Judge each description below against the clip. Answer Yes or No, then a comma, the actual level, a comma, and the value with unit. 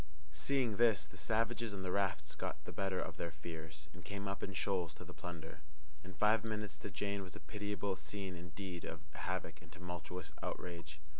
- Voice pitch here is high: No, very low, 95 Hz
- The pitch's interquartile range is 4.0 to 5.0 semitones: No, average, 3.4 semitones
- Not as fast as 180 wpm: No, average, 195 wpm